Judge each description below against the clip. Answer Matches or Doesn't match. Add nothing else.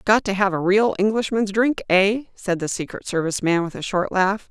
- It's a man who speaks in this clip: Doesn't match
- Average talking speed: Doesn't match